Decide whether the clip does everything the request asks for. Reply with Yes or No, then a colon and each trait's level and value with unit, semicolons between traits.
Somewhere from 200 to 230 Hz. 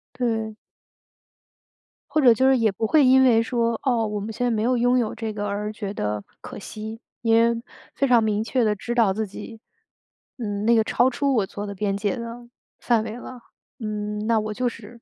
Yes: high, 225 Hz